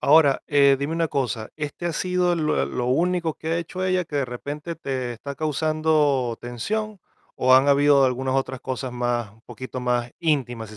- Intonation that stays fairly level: No, average, 4.2 semitones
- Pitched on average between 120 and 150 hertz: Yes, medium, 140 Hz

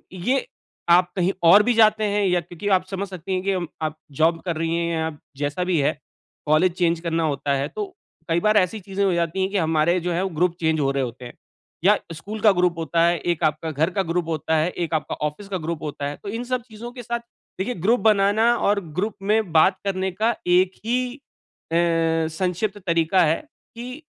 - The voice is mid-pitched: Yes, medium, 180 Hz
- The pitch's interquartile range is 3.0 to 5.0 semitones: Yes, average, 4.0 semitones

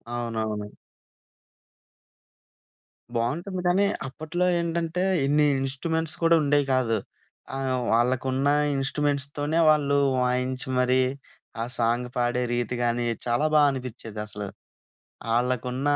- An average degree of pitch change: Yes, average, 3.7 semitones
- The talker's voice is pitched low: Yes, low, 130 Hz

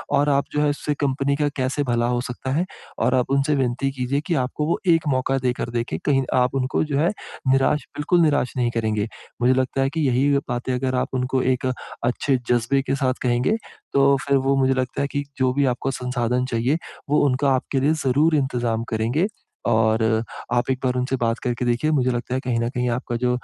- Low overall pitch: Yes, low, 130 Hz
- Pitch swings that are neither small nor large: No, narrow, 2.2 semitones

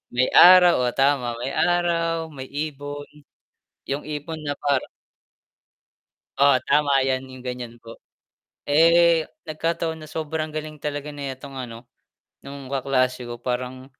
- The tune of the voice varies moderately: Yes, average, 3.1 semitones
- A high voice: No, medium, 140 Hz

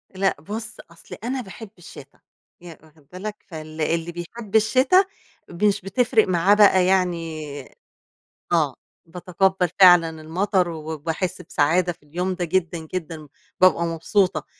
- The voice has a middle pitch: Yes, medium, 180 Hz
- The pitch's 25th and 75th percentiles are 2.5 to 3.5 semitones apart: Yes, average, 3.1 semitones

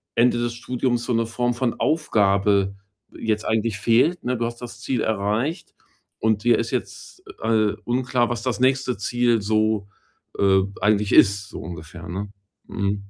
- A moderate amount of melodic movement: Yes, average, 3.0 semitones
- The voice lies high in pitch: No, low, 115 Hz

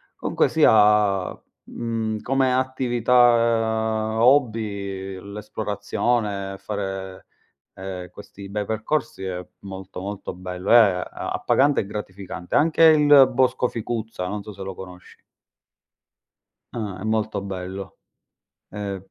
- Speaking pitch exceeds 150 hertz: No, low, 105 Hz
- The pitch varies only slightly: No, average, 3.2 semitones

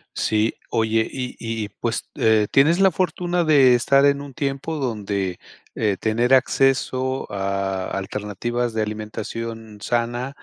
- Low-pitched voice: Yes, low, 115 Hz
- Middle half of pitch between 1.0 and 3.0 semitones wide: No, average, 4.0 semitones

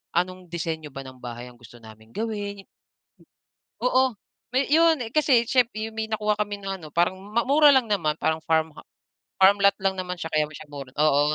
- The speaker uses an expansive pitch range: Yes, wide, 6.2 semitones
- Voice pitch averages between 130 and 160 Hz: No, high, 190 Hz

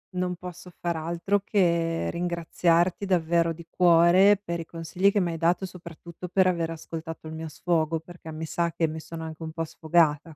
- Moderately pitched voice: Yes, medium, 170 Hz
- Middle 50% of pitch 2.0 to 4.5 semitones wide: No, narrow, 1.6 semitones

